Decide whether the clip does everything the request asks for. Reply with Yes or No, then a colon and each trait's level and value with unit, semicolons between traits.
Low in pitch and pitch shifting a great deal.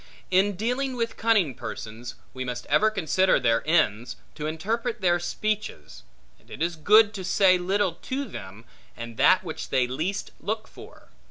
No: medium, 180 Hz; wide, 8.7 semitones